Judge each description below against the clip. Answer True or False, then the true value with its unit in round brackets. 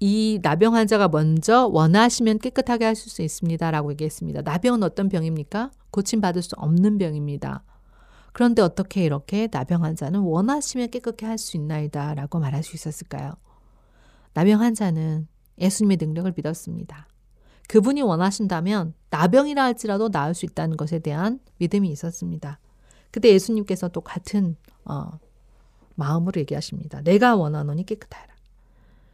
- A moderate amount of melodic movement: False (5.7 semitones)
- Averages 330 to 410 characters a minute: True (350 characters per minute)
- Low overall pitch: False (175 Hz)